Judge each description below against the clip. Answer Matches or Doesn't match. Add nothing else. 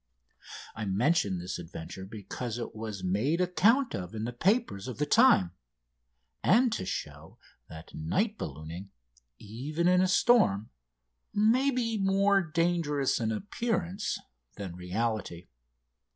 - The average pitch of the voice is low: Matches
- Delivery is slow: Matches